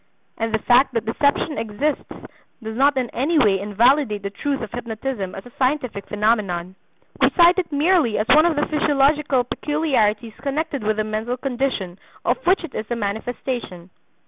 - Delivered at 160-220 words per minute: Yes, average, 170 wpm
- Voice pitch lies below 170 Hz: No, high, 245 Hz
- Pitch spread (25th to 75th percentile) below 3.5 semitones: No, average, 5.3 semitones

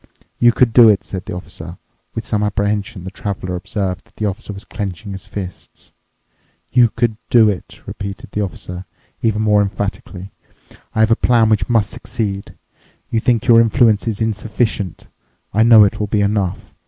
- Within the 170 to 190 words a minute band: Yes, average, 175 wpm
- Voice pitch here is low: Yes, low, 105 Hz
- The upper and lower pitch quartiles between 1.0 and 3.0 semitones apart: Yes, narrow, 2.5 semitones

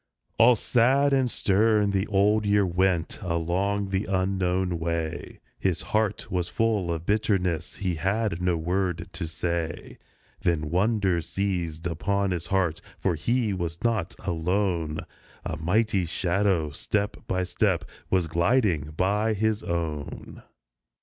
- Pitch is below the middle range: Yes, very low, 95 Hz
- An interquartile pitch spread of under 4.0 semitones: Yes, average, 3.3 semitones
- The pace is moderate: No, slow, 130 wpm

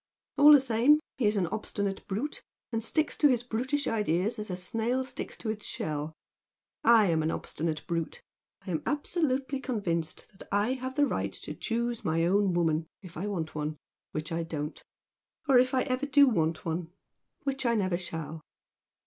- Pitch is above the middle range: Yes, high, 210 Hz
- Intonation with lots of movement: Yes, wide, 7.5 semitones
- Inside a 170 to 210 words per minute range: Yes, average, 185 wpm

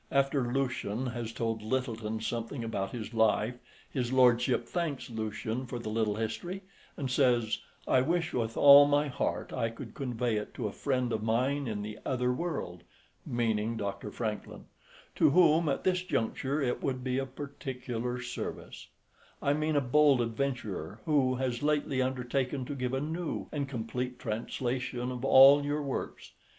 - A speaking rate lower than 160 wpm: No, average, 165 wpm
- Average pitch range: Yes, average, 3.5 semitones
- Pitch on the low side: Yes, low, 125 Hz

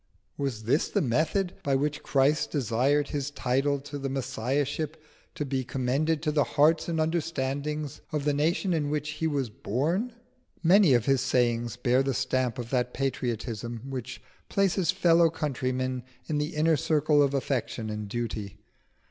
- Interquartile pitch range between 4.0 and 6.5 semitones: No, average, 3.3 semitones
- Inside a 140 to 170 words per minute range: Yes, average, 160 wpm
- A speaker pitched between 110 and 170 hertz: Yes, medium, 140 Hz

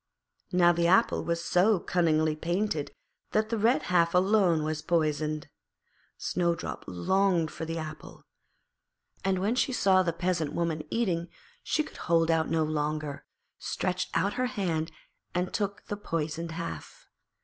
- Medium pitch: Yes, medium, 170 Hz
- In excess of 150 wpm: No, average, 145 wpm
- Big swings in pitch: No, average, 3.3 semitones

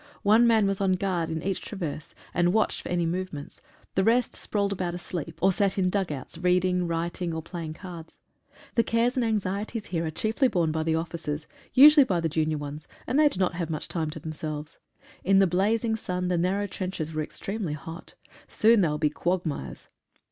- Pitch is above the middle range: No, medium, 180 Hz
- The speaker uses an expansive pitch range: No, average, 3.7 semitones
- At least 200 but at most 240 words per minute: Yes, fast, 205 wpm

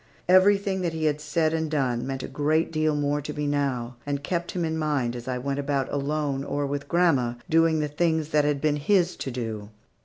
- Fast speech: Yes, fast, 220 wpm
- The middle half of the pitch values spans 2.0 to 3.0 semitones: Yes, narrow, 2.6 semitones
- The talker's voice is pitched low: No, medium, 150 Hz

